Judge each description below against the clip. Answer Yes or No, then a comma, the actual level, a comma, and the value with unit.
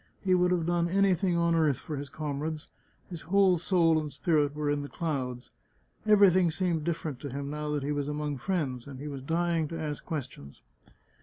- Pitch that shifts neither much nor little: Yes, average, 3.2 semitones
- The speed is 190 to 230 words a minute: Yes, average, 200 wpm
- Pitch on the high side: No, medium, 155 Hz